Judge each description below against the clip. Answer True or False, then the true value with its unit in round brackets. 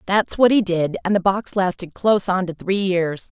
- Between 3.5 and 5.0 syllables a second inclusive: True (4.9 syllables/s)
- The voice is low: False (190 Hz)